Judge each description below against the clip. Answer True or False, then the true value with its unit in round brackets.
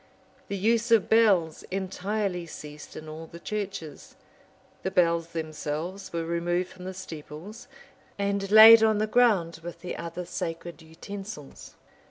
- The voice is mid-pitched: True (180 Hz)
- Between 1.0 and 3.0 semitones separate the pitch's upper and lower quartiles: False (3.6 semitones)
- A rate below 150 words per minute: True (140 wpm)